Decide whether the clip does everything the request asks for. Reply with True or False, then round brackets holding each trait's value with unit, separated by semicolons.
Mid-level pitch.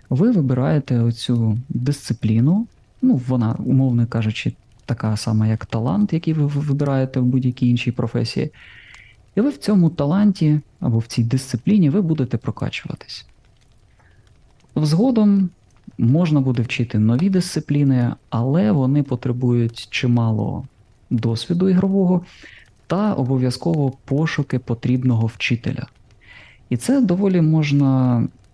False (130 Hz)